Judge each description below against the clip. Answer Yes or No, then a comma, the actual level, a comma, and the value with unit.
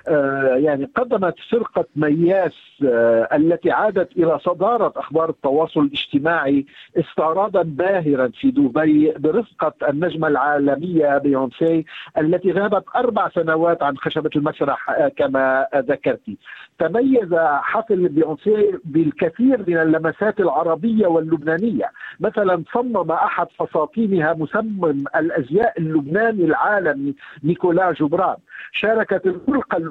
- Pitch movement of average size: Yes, average, 4.7 semitones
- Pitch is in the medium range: Yes, medium, 165 Hz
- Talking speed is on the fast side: No, average, 100 wpm